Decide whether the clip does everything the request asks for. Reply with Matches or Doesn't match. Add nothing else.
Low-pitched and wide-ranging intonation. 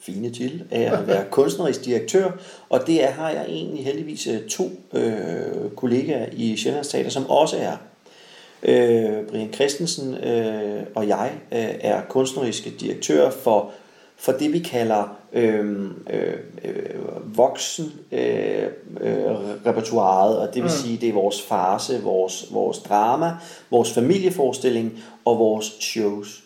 Matches